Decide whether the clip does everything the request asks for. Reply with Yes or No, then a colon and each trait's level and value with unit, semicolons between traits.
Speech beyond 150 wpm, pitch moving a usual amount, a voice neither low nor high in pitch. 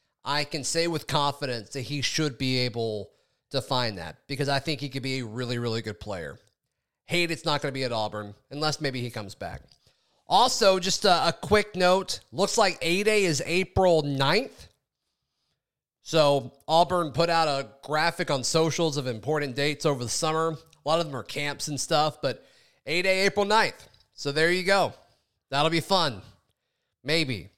Yes: average, 185 wpm; average, 4.6 semitones; medium, 145 Hz